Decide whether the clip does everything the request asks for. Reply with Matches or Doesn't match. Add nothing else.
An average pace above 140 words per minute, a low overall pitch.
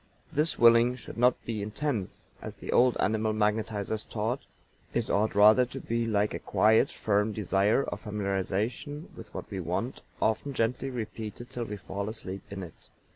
Matches